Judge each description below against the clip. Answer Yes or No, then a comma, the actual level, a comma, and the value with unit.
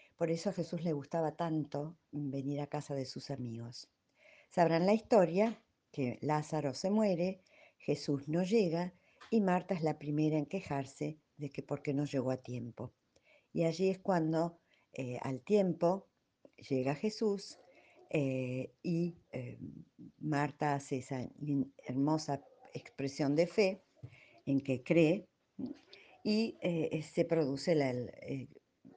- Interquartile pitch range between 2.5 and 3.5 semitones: No, average, 4.2 semitones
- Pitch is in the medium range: Yes, medium, 155 Hz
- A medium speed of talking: Yes, average, 135 wpm